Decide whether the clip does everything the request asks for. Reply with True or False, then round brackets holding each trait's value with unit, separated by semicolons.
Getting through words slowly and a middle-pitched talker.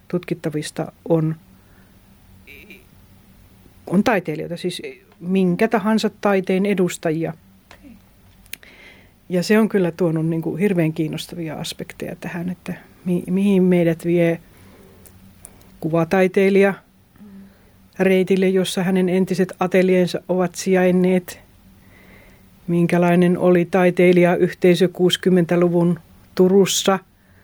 True (85 wpm; 175 Hz)